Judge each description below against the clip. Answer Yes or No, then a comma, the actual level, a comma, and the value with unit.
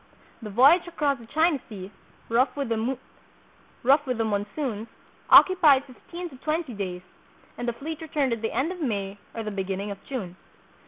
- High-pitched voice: Yes, high, 245 Hz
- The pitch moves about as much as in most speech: No, wide, 5.8 semitones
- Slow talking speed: No, average, 160 wpm